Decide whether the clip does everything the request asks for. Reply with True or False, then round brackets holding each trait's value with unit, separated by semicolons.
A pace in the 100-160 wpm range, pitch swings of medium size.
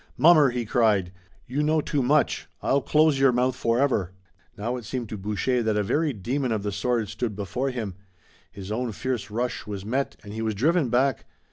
False (200 wpm; 4.2 semitones)